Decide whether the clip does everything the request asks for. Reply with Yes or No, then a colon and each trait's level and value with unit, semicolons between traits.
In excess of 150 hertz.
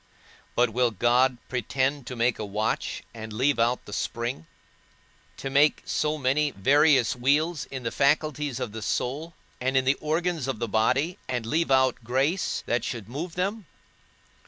No: low, 130 Hz